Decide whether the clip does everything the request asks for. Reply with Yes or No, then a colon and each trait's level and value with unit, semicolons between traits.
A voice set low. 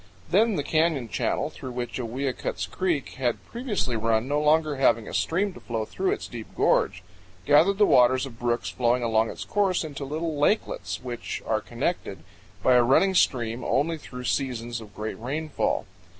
Yes: low, 130 Hz